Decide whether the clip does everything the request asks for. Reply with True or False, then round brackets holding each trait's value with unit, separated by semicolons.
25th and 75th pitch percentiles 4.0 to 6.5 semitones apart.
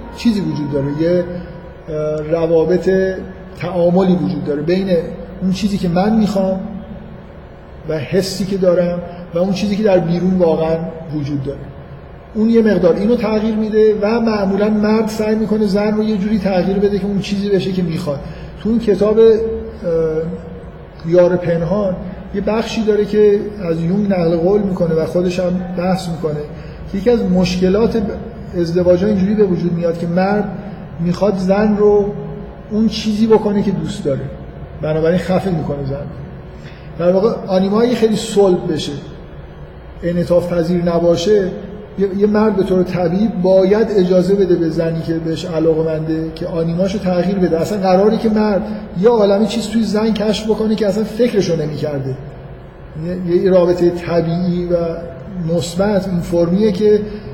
False (3.3 semitones)